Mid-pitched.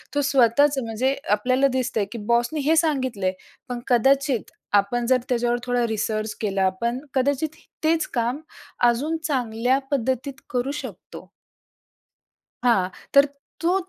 No: very high, 250 Hz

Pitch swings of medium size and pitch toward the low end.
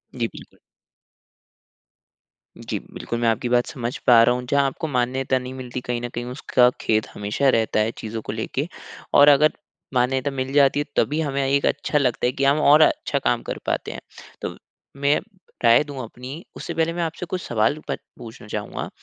Yes: average, 3.0 semitones; low, 130 Hz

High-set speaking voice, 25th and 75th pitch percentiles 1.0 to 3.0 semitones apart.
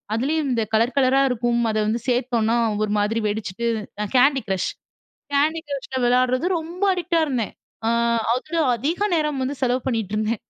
No: very high, 250 Hz; average, 4.0 semitones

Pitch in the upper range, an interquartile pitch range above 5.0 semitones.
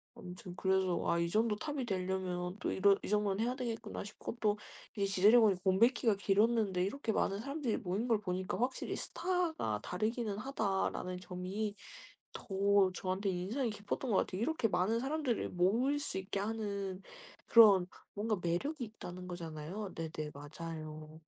No: high, 200 Hz; average, 3.9 semitones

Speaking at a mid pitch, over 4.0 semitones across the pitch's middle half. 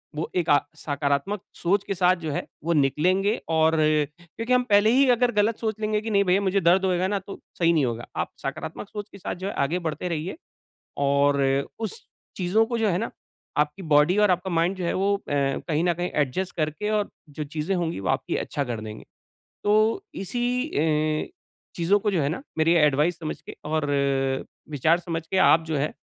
Yes: medium, 175 Hz; average, 4.9 semitones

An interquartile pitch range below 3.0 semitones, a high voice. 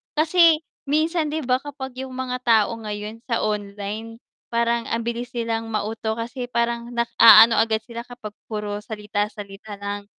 Yes: narrow, 2.6 semitones; high, 230 Hz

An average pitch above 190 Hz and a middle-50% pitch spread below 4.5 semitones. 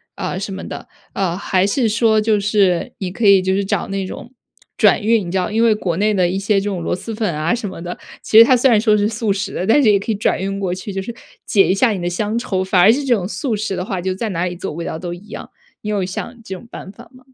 Yes: high, 200 Hz; average, 3.0 semitones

